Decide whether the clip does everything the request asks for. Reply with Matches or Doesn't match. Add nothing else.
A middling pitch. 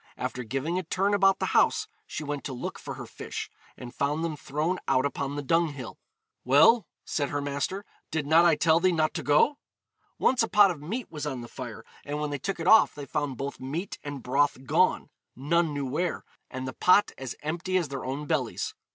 Matches